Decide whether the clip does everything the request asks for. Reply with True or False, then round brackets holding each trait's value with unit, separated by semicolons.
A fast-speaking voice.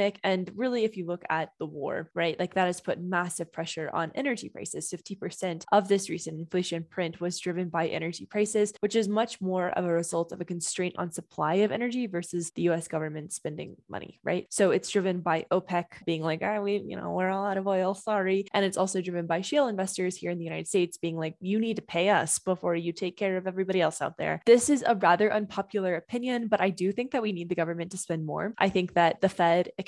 True (235 wpm)